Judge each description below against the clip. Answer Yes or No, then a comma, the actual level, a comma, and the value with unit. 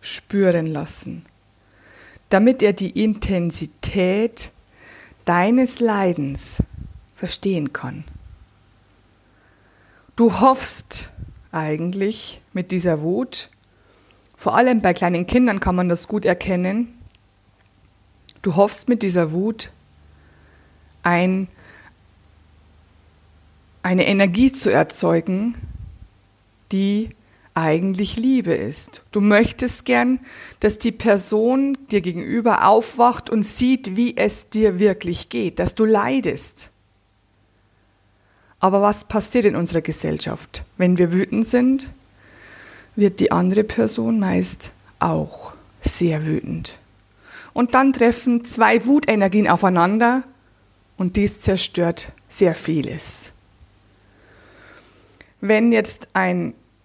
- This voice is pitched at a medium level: Yes, medium, 175 Hz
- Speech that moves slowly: Yes, slow, 95 wpm